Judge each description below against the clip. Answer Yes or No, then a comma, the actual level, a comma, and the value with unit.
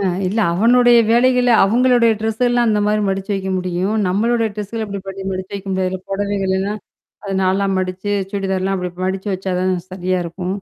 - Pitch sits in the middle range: No, high, 195 Hz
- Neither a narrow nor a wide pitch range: Yes, average, 3.0 semitones